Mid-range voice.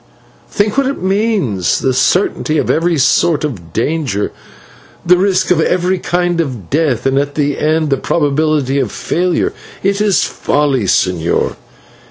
Yes: medium, 155 Hz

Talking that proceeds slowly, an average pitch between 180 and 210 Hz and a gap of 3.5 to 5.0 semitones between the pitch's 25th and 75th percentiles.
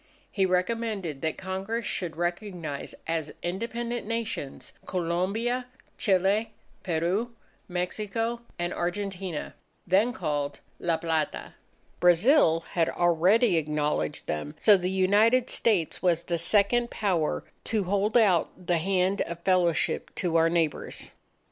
Yes: slow, 115 wpm; medium, 185 Hz; average, 4.2 semitones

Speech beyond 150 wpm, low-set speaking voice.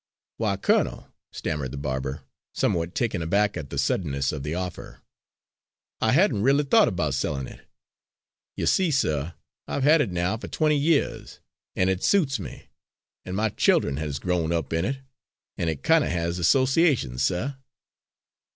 Yes: average, 160 wpm; very low, 90 Hz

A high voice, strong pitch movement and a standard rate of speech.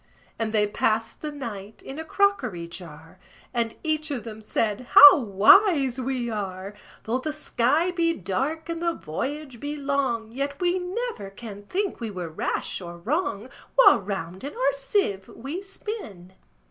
Yes: very high, 250 Hz; wide, 7.3 semitones; average, 160 wpm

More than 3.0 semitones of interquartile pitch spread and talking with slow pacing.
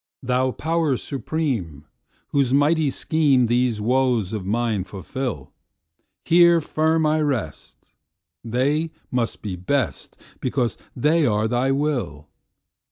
Yes: average, 5.1 semitones; slow, 100 wpm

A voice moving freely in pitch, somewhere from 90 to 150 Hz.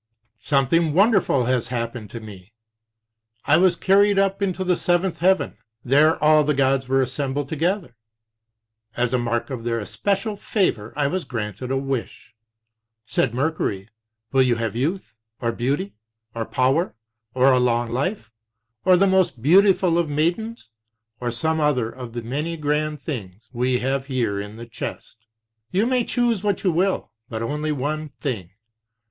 Yes: wide, 6.6 semitones; medium, 140 Hz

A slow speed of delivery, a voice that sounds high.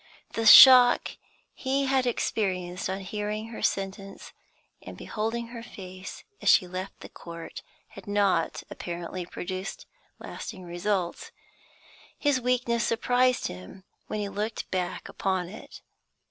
Yes: slow, 125 wpm; high, 205 Hz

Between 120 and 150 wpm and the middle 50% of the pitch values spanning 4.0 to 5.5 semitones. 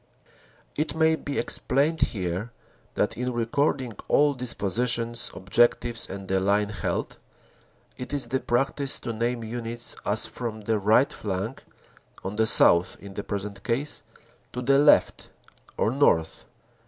Yes: average, 140 wpm; average, 4.4 semitones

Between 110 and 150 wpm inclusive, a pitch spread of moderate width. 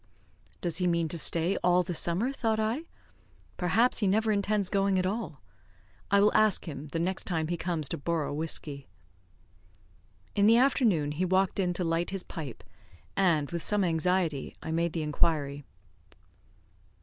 No: average, 165 wpm; average, 3.7 semitones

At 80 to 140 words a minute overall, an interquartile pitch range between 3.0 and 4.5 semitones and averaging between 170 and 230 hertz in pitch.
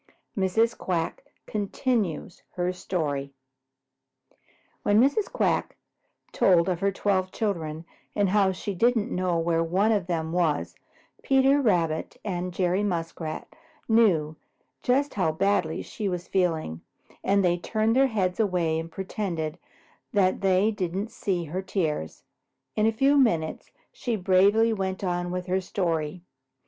Yes: slow, 135 wpm; average, 3.7 semitones; medium, 185 Hz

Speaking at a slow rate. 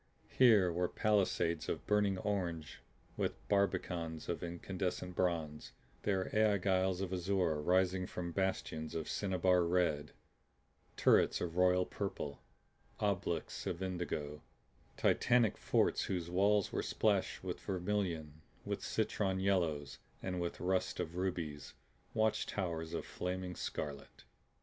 Yes: slow, 120 wpm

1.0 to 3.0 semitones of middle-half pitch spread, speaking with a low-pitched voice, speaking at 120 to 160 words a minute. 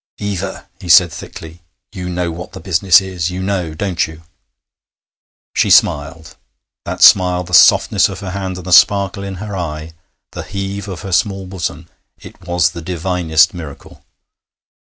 Yes: narrow, 2.5 semitones; very low, 90 Hz; average, 155 wpm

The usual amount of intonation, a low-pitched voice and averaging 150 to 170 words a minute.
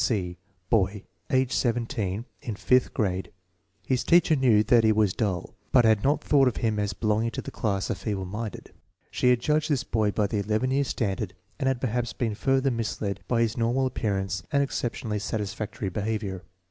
No: average, 3.7 semitones; low, 110 Hz; average, 190 wpm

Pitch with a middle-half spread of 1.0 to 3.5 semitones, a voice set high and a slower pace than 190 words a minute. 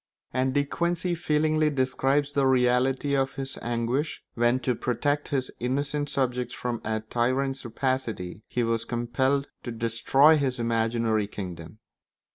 No: average, 3.1 semitones; low, 130 Hz; slow, 135 wpm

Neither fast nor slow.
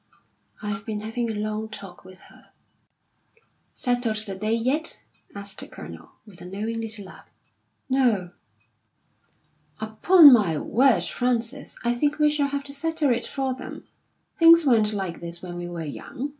Yes: average, 155 wpm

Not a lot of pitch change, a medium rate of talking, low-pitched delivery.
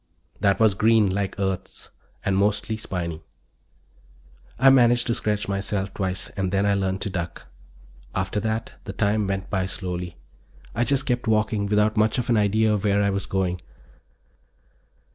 Yes: narrow, 2.3 semitones; average, 160 wpm; low, 100 Hz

